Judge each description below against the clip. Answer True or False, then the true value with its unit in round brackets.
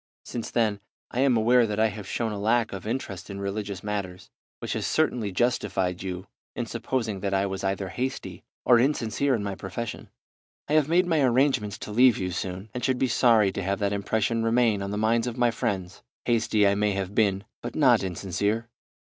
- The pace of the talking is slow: False (205 wpm)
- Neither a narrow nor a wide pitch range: True (3.5 semitones)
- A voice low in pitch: True (110 Hz)